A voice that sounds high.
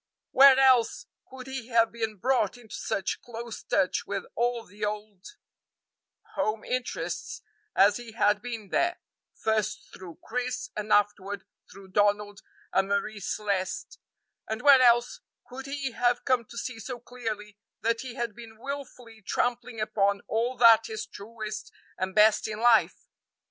Yes: high, 225 Hz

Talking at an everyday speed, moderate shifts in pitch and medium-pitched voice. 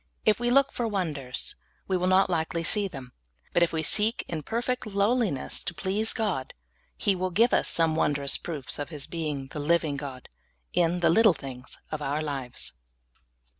No: average, 180 wpm; wide, 5.8 semitones; medium, 170 Hz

